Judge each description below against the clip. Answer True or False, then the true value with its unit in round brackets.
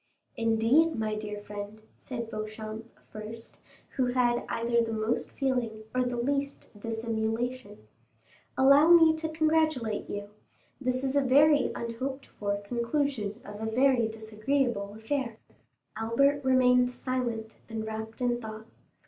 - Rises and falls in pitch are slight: False (3.3 semitones)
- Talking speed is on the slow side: True (130 wpm)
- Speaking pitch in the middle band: False (235 Hz)